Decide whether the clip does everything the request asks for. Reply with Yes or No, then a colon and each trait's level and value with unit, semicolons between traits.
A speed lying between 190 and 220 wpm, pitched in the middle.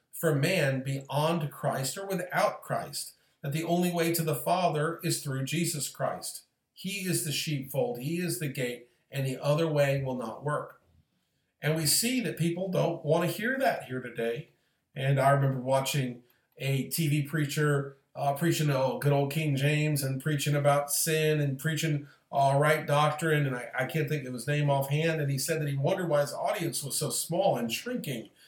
Yes: average, 195 wpm; medium, 150 Hz